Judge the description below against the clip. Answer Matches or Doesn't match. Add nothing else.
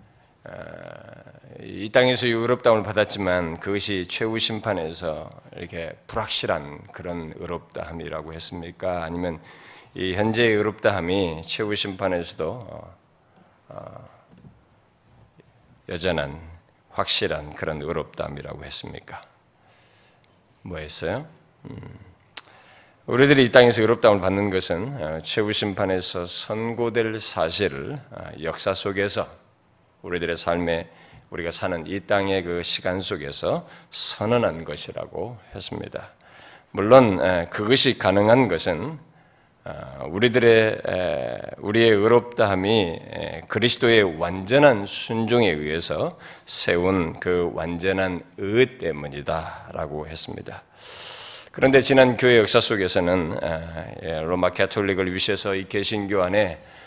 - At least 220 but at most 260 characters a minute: Matches